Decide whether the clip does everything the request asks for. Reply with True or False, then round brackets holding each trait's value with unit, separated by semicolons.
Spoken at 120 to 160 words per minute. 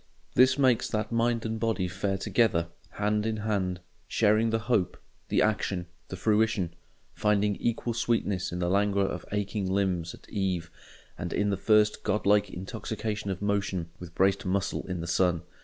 False (170 wpm)